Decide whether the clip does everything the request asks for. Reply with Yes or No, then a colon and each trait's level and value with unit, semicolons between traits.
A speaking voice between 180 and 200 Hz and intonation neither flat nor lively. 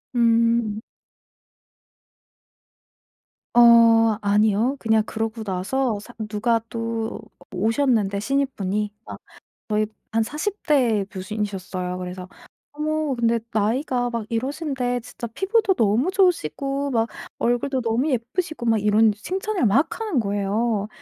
No: high, 230 Hz; average, 4.1 semitones